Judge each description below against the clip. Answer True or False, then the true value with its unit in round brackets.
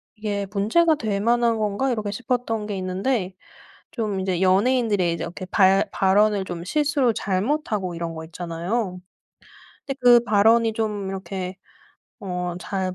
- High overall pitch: True (205 Hz)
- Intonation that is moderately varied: True (3.7 semitones)